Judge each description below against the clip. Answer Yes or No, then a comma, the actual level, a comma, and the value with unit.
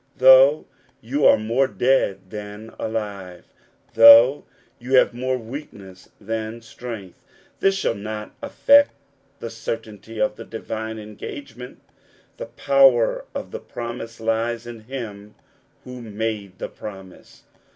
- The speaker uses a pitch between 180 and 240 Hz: No, low, 115 Hz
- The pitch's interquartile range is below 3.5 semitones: Yes, average, 2.9 semitones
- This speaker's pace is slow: Yes, slow, 120 wpm